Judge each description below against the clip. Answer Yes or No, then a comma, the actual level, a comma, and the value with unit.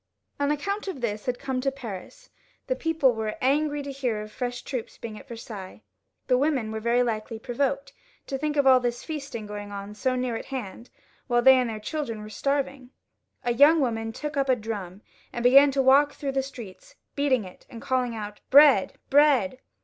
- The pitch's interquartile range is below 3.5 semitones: No, average, 4.0 semitones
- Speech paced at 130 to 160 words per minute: No, fast, 205 wpm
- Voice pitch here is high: Yes, very high, 255 Hz